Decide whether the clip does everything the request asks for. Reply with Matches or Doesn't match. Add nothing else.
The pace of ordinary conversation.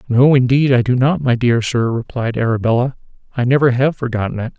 Matches